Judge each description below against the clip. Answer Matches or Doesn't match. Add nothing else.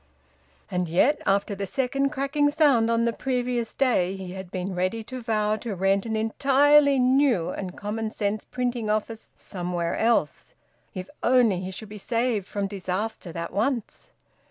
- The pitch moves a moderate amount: Matches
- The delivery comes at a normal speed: Matches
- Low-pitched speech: Doesn't match